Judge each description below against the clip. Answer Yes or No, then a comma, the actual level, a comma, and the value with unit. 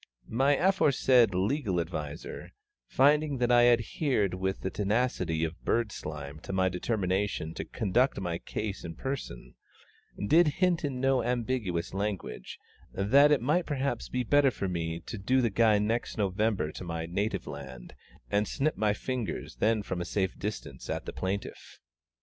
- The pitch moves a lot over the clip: Yes, wide, 5.8 semitones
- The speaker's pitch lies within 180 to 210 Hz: No, low, 105 Hz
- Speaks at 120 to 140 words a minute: No, average, 160 wpm